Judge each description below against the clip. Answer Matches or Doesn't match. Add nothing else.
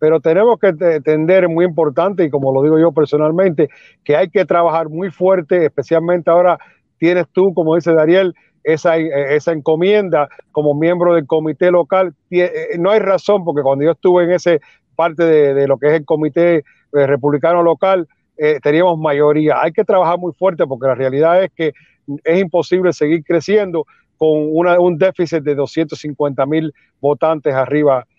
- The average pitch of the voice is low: Doesn't match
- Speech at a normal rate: Matches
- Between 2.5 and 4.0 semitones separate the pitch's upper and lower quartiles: Matches